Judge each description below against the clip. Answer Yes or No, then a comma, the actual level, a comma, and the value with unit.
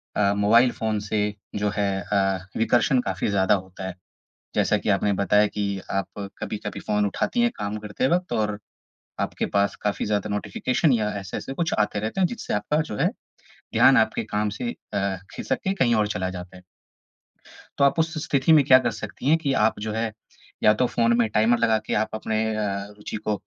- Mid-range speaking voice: No, low, 105 Hz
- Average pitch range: Yes, average, 3.1 semitones